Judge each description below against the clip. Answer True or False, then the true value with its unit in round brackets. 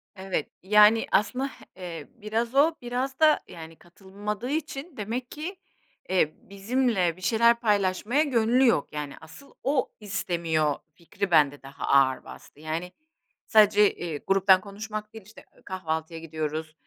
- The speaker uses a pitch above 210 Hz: False (200 Hz)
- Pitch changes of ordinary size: False (6.1 semitones)